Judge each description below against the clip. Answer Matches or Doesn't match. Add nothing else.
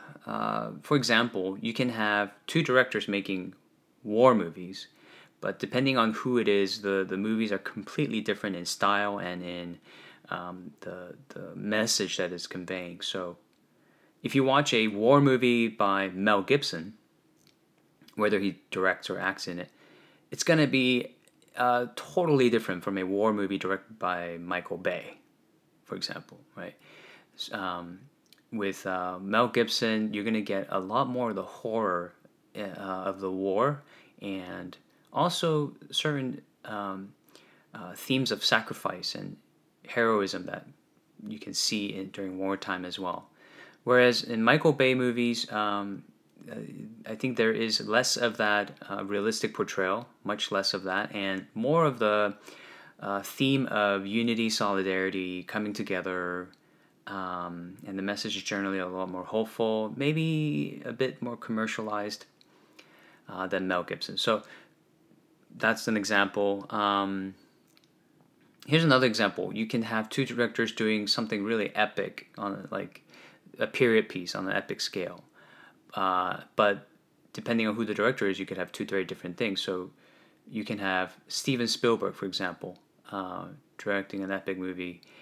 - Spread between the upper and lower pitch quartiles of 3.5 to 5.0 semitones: Matches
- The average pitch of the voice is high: Doesn't match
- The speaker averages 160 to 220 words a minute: Doesn't match